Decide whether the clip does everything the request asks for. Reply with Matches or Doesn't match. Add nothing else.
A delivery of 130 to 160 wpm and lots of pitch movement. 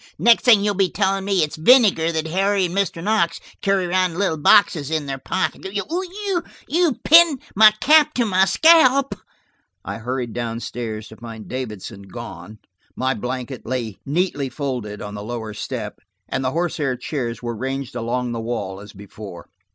Doesn't match